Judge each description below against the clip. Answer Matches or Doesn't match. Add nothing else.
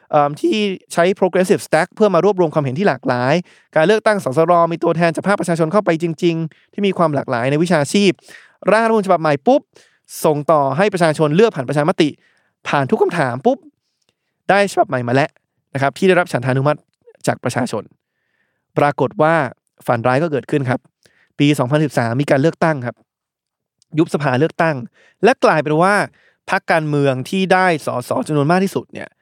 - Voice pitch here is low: Doesn't match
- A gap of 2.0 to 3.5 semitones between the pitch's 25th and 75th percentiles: Doesn't match